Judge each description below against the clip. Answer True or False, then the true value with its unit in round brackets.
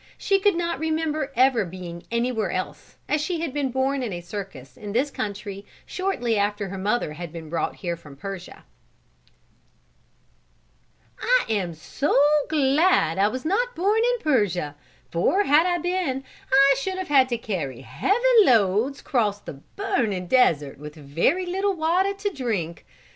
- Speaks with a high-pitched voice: True (245 Hz)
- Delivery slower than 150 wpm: False (160 wpm)